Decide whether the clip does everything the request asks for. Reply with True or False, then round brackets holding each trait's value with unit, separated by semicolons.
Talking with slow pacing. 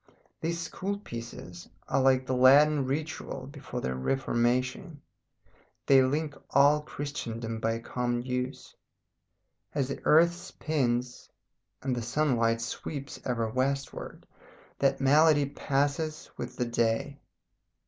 True (115 wpm)